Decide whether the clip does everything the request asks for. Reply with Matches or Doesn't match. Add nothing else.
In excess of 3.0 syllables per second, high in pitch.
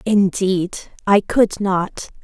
Doesn't match